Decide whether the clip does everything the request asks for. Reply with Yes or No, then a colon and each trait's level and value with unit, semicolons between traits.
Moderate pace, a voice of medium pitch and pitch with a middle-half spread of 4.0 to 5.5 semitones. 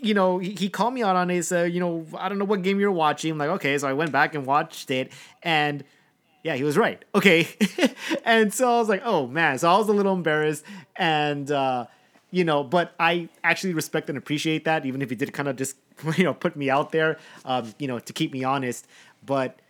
No: fast, 240 wpm; medium, 160 Hz; average, 4.8 semitones